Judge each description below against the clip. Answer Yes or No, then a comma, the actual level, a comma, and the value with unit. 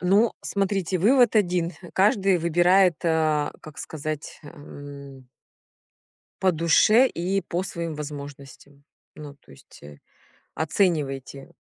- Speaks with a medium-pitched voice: Yes, medium, 165 Hz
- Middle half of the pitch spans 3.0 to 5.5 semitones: Yes, average, 4.7 semitones